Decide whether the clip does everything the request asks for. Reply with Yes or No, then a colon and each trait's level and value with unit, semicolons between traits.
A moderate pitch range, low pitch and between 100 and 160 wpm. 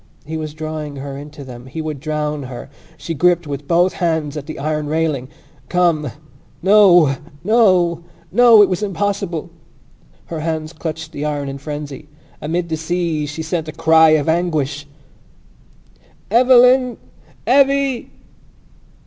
No: average, 3.1 semitones; medium, 160 Hz; average, 140 wpm